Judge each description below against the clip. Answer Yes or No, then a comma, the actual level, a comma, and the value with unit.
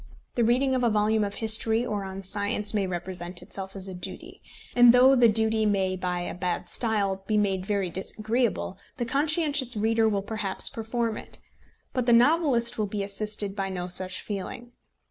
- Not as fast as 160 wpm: No, average, 185 wpm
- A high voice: Yes, high, 210 Hz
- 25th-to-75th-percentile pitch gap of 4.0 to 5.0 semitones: No, average, 3.4 semitones